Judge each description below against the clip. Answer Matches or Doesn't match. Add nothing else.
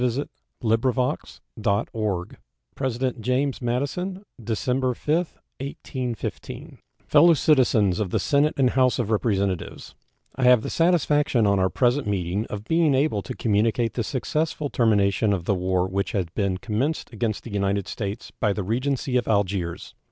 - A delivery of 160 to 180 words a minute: Doesn't match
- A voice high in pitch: Doesn't match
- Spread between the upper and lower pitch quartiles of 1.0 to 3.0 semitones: Doesn't match